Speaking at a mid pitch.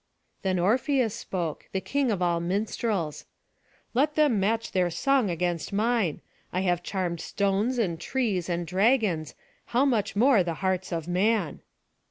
No: high, 195 Hz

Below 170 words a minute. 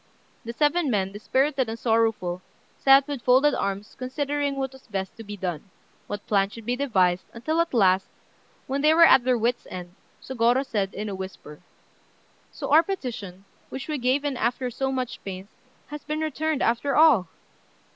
No: average, 175 wpm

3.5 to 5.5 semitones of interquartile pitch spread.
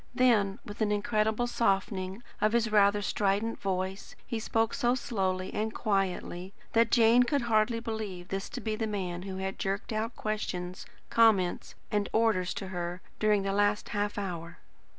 No: average, 2.7 semitones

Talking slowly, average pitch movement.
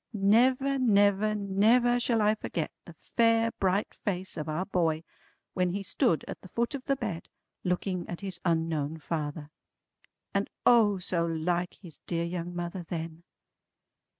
No: average, 150 wpm; average, 4.3 semitones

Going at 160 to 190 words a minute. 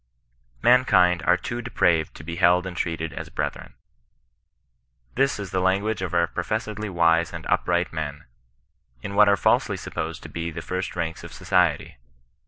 Yes: average, 175 wpm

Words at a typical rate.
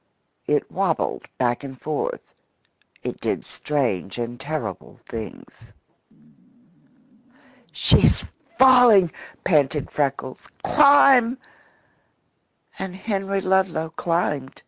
No: slow, 80 wpm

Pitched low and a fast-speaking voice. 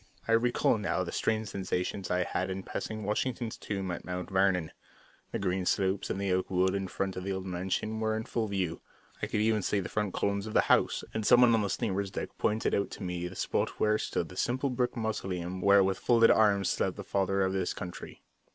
Yes: low, 100 Hz; fast, 225 wpm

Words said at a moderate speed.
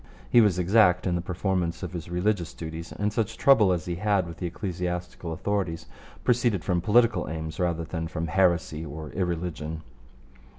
Yes: average, 170 wpm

